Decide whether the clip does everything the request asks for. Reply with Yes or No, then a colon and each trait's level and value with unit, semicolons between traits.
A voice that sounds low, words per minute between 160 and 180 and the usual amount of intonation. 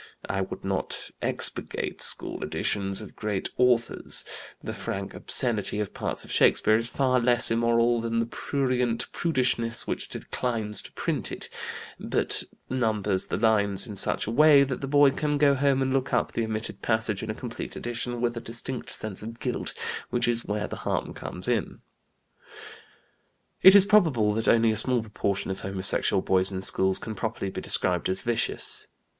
Yes: low, 115 Hz; average, 175 wpm; average, 3.1 semitones